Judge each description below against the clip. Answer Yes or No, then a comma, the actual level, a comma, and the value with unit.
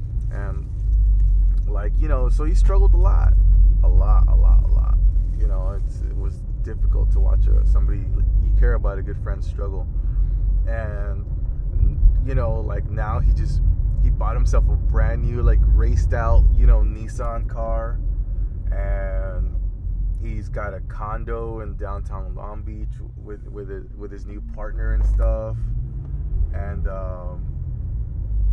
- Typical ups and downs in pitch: Yes, average, 3.4 semitones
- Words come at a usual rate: Yes, average, 150 wpm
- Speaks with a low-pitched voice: Yes, very low, 95 Hz